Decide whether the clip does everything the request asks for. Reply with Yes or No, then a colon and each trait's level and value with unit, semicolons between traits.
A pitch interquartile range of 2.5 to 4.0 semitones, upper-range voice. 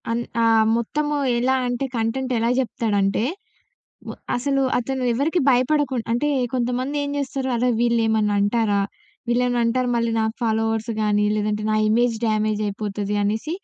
Yes: average, 2.9 semitones; high, 235 Hz